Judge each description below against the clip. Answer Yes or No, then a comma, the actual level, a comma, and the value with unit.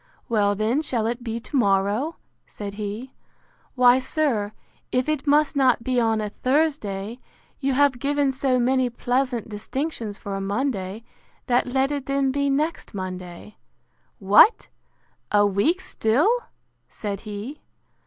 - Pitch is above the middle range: Yes, high, 245 Hz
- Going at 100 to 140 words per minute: Yes, slow, 135 wpm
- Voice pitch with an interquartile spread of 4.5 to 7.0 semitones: Yes, average, 4.9 semitones